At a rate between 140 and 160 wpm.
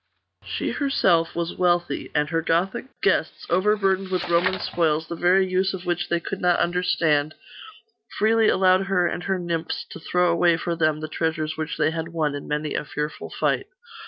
No: average, 185 wpm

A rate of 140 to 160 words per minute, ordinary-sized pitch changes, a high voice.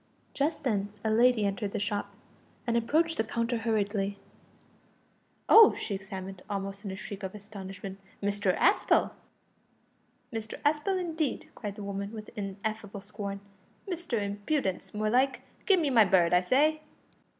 Yes: average, 145 wpm; average, 4.1 semitones; high, 210 Hz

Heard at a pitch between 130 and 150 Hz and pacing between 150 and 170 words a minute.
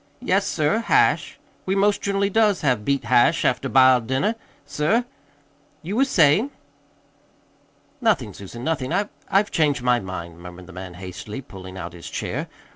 Yes: low, 135 Hz; average, 155 wpm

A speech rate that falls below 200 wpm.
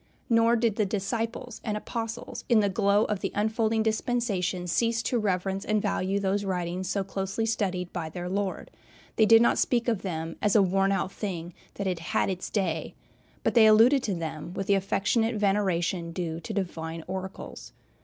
Yes: average, 185 wpm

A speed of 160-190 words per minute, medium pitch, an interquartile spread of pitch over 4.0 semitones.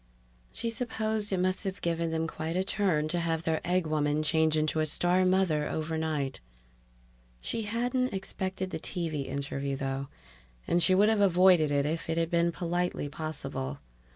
No: average, 170 wpm; medium, 165 Hz; average, 3.3 semitones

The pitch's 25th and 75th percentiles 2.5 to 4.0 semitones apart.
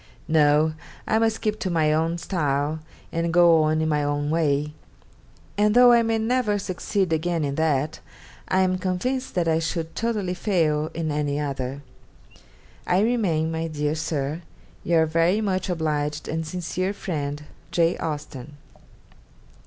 Yes: average, 3.7 semitones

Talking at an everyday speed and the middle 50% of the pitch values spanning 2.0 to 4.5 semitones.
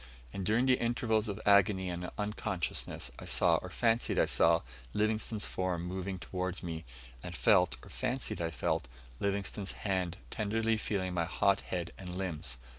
Yes: average, 160 wpm; average, 3.2 semitones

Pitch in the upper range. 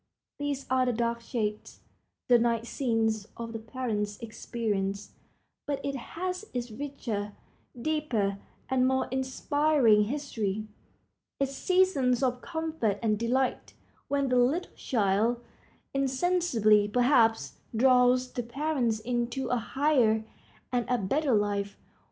Yes: high, 245 Hz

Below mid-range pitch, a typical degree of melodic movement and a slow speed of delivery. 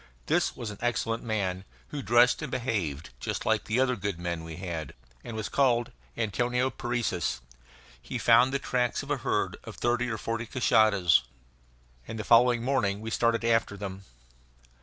No: low, 115 Hz; average, 3.7 semitones; average, 170 wpm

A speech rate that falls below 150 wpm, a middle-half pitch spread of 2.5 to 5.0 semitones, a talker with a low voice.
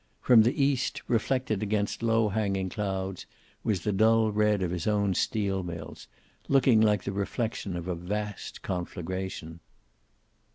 Yes: average, 140 wpm; average, 2.9 semitones; low, 105 Hz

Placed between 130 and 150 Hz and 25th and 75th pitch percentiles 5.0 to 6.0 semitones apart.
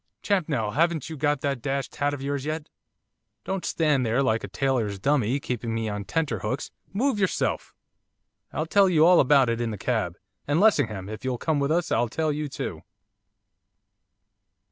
Yes: medium, 140 Hz; wide, 5.4 semitones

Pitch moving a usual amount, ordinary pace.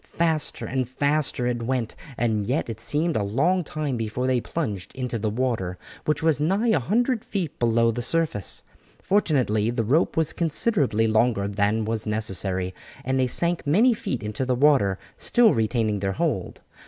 No: wide, 6.1 semitones; average, 170 wpm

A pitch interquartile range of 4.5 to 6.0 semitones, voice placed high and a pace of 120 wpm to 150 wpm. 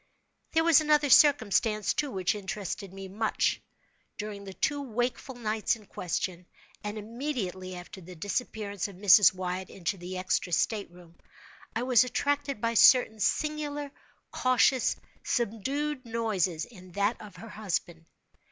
Yes: average, 5.2 semitones; high, 215 Hz; average, 140 wpm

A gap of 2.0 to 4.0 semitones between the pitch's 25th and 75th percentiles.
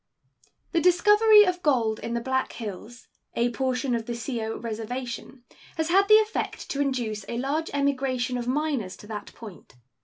No: average, 4.6 semitones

